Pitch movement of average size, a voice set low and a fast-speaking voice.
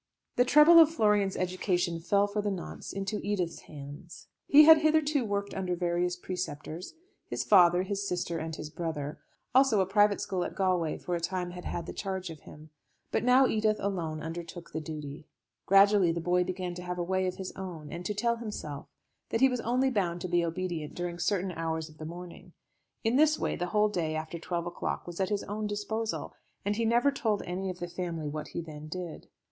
No: average, 3.6 semitones; medium, 180 Hz; fast, 210 wpm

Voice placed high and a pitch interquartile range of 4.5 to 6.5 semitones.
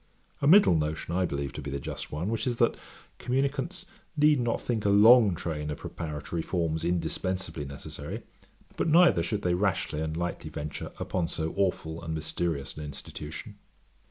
No: very low, 85 Hz; wide, 5.4 semitones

